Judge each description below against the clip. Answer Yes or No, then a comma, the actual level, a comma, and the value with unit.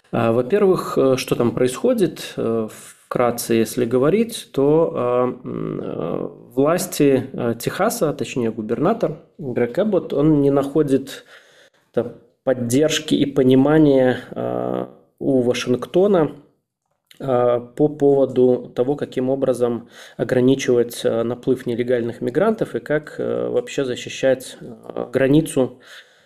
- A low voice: Yes, low, 130 Hz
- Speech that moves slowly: Yes, slow, 80 wpm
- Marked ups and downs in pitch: No, average, 3.1 semitones